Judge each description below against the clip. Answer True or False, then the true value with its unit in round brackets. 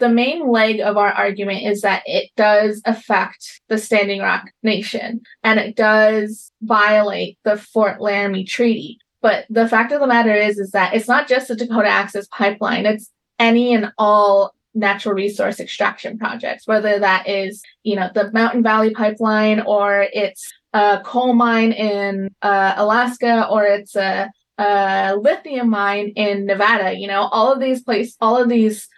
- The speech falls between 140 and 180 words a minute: True (170 wpm)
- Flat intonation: True (2.2 semitones)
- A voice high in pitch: True (215 Hz)